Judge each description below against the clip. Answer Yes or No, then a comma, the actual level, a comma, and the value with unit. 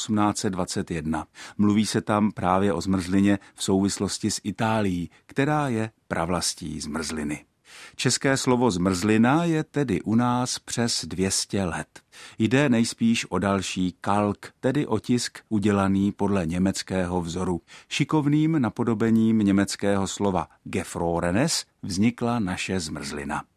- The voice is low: Yes, low, 100 Hz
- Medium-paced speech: No, slow, 110 wpm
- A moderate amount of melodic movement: Yes, average, 3.9 semitones